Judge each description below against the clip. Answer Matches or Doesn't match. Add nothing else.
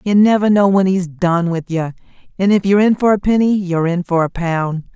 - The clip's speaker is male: Doesn't match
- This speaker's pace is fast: Matches